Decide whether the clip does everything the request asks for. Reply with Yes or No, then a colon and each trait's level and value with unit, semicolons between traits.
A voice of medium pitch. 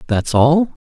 Yes: medium, 145 Hz